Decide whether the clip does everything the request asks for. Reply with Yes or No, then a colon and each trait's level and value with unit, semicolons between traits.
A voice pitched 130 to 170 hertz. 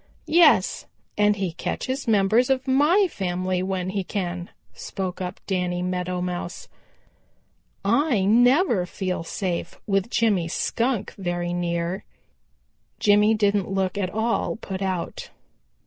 No: high, 195 Hz